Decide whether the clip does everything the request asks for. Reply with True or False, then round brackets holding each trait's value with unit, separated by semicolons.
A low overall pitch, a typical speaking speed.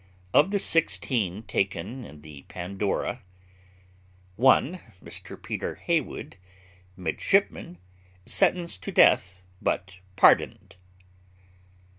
False (95 Hz; 90 wpm)